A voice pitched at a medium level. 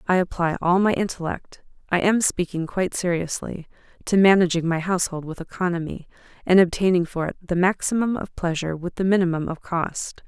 Yes: medium, 180 Hz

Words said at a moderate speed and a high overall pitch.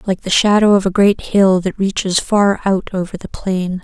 No: fast, 220 wpm; high, 195 Hz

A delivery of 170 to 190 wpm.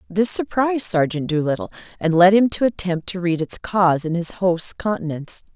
Yes: average, 185 wpm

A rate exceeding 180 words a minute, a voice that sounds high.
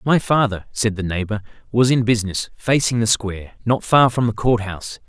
No: average, 200 wpm; low, 110 Hz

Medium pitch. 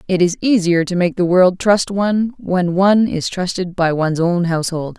Yes: medium, 180 Hz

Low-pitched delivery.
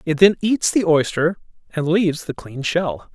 No: medium, 165 Hz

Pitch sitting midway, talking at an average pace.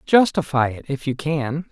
Yes: medium, 150 Hz; average, 175 wpm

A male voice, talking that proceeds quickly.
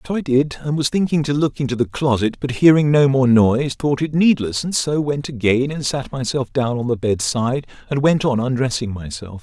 Yes: male; fast, 230 wpm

